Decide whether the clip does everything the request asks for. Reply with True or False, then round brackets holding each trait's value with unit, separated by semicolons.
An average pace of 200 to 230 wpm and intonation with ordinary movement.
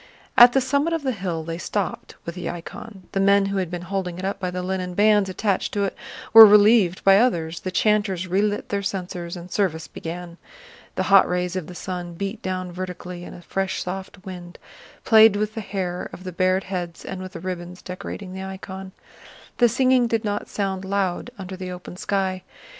False (205 wpm; 2.1 semitones)